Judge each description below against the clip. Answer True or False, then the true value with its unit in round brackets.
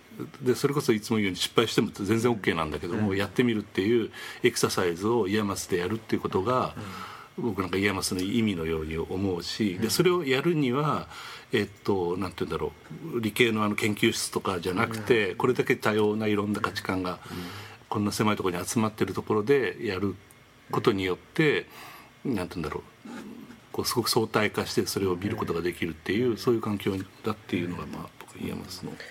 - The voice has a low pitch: True (105 Hz)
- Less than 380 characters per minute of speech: False (425 characters per minute)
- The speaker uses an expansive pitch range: False (3.3 semitones)